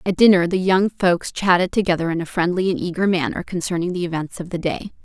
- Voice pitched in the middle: Yes, medium, 180 Hz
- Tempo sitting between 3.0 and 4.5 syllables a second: No, 6.0 syllables/s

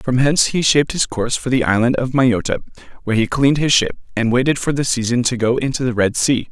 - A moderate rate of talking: No, fast, 250 wpm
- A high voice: No, low, 130 Hz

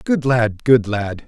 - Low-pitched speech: Yes, low, 120 Hz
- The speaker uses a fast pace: No, average, 190 wpm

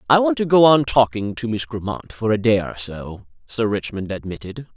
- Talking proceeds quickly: Yes, fast, 215 wpm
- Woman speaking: No, male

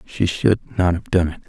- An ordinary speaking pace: No, fast, 245 wpm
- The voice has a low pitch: Yes, very low, 90 Hz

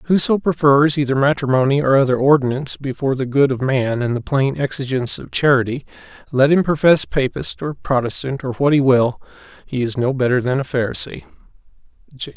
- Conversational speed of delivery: Yes, average, 170 wpm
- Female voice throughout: No, male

